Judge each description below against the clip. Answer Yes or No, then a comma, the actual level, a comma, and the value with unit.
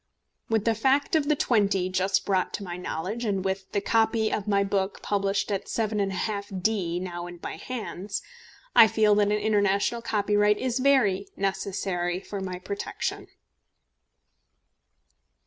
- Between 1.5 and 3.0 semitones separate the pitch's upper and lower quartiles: Yes, narrow, 2.4 semitones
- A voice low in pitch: No, high, 200 Hz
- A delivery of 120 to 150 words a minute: Yes, average, 145 wpm